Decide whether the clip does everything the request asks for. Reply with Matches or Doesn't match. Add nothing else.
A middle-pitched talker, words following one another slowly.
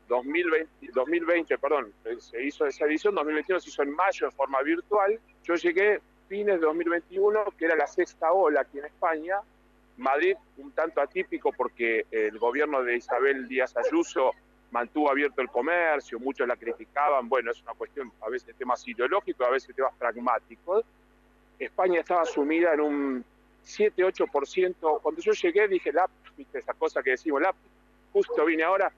Doesn't match